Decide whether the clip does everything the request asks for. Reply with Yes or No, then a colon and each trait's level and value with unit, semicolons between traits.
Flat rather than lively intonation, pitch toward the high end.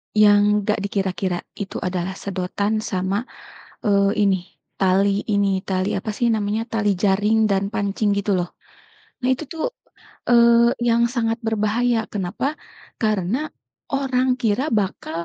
No: average, 3.1 semitones; high, 210 Hz